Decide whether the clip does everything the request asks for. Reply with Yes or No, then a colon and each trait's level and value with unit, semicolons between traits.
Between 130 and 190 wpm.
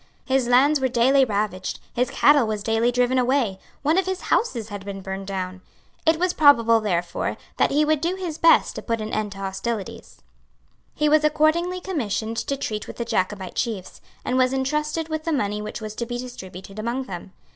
No: average, 200 wpm